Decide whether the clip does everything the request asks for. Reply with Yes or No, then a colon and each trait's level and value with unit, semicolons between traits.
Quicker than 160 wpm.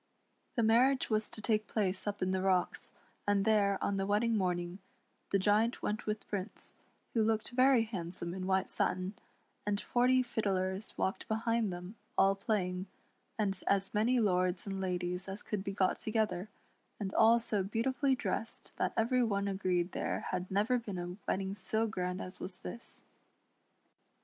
Yes: average, 170 wpm